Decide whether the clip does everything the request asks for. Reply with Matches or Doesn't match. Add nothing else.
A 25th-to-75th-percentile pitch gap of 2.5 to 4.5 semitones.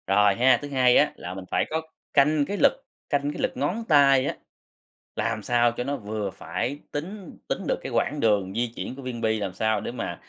Doesn't match